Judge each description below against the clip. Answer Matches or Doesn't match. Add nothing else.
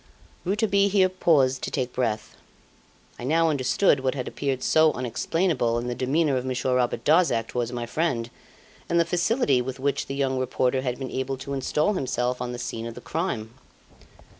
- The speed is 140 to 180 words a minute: Doesn't match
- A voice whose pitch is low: Matches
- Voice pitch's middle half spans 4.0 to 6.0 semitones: Matches